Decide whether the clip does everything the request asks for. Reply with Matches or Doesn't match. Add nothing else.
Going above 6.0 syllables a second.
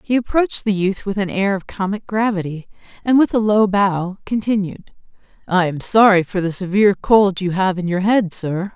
Doesn't match